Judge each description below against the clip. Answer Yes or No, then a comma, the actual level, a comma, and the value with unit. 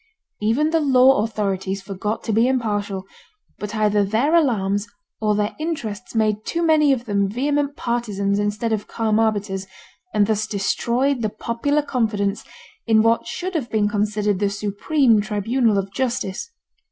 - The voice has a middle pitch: No, high, 215 Hz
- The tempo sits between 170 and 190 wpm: No, average, 155 wpm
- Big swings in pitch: No, average, 3.6 semitones